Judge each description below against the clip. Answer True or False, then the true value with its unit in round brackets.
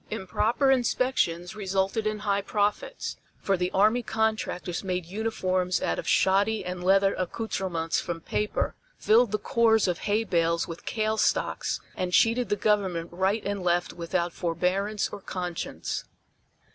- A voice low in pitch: False (195 Hz)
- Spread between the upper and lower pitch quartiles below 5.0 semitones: True (3.3 semitones)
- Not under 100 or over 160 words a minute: True (145 wpm)